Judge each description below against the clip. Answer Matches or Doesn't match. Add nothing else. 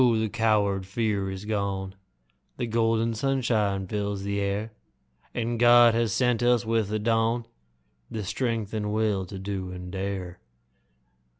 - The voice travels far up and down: Doesn't match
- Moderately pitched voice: Doesn't match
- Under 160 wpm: Matches